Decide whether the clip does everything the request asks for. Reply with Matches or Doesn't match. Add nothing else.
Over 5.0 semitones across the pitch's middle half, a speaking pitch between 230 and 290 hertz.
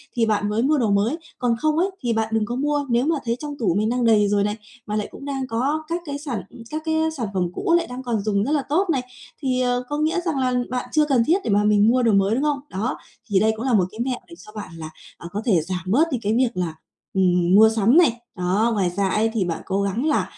Matches